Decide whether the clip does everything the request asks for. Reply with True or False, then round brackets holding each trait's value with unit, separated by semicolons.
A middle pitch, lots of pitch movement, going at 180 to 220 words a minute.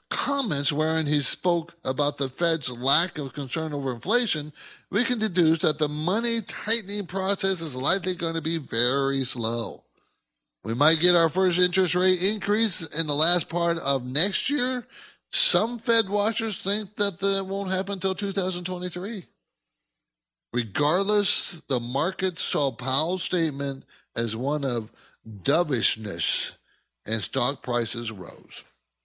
False (165 Hz; 6.4 semitones; 135 wpm)